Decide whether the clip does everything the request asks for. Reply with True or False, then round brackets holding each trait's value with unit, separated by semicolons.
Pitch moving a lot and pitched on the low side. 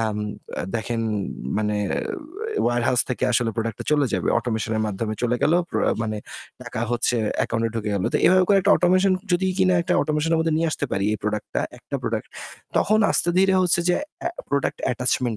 True (7.5 semitones; 120 Hz)